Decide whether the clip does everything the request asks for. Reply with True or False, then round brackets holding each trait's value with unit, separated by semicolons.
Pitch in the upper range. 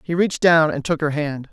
False (155 Hz)